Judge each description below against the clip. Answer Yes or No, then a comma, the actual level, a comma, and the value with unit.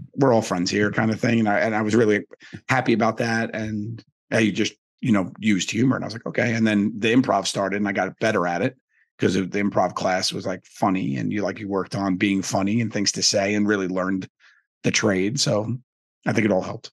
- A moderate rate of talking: No, fast, 250 wpm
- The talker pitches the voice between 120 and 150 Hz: No, low, 105 Hz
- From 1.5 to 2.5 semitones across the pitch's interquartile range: Yes, narrow, 2.2 semitones